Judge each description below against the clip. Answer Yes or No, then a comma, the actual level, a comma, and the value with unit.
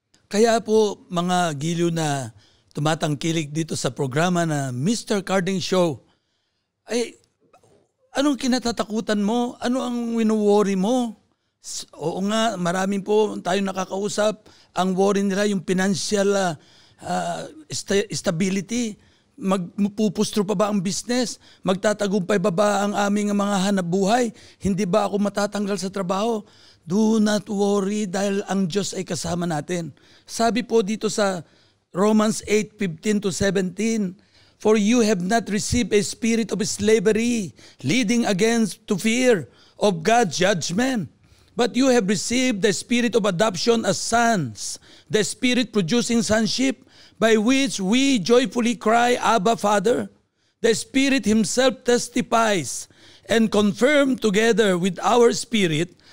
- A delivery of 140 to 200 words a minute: No, average, 125 wpm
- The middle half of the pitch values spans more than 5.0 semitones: No, average, 3.5 semitones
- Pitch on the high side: Yes, high, 210 Hz